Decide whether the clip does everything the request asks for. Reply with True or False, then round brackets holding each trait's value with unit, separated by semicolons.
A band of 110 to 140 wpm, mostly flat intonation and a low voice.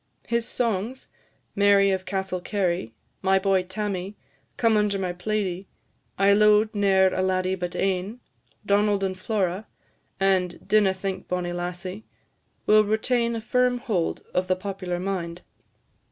False (135 wpm; 2.3 semitones; 195 Hz)